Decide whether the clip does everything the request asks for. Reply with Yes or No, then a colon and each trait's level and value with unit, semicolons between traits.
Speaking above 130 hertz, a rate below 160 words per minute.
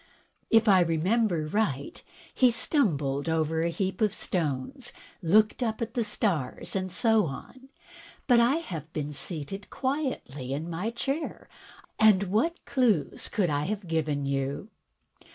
Yes: medium, 185 Hz; average, 140 wpm